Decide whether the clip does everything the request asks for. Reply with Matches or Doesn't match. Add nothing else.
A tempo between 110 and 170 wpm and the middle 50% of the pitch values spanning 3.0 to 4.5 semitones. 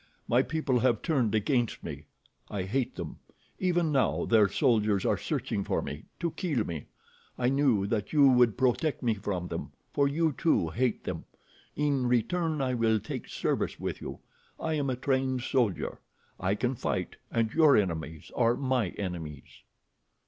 Doesn't match